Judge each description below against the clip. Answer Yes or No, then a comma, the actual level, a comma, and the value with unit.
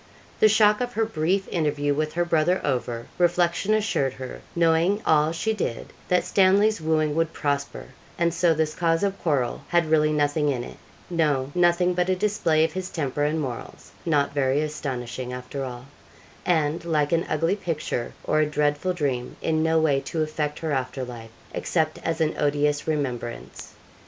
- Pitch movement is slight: No, average, 3.2 semitones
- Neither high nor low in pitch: Yes, medium, 155 Hz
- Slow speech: No, average, 175 wpm